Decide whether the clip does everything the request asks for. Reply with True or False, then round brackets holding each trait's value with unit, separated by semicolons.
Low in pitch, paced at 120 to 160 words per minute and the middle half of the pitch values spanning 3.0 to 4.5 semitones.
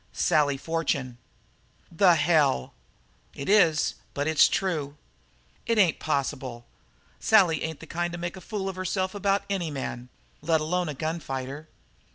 False (160 Hz; 150 wpm; 4.1 semitones)